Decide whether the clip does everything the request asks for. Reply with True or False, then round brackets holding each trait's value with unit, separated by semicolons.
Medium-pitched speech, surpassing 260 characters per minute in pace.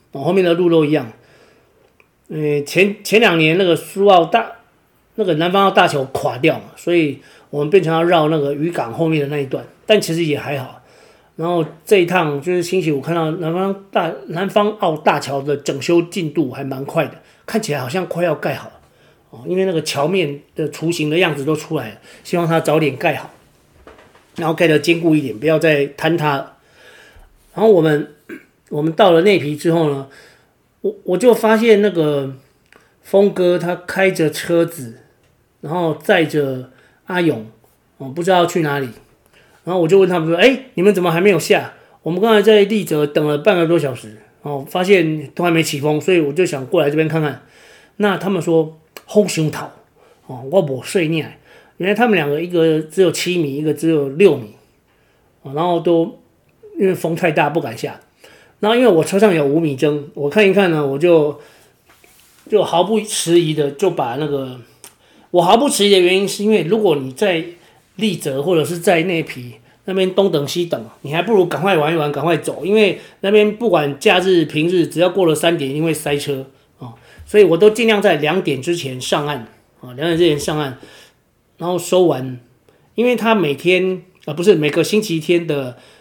True (165 Hz; 270 characters per minute)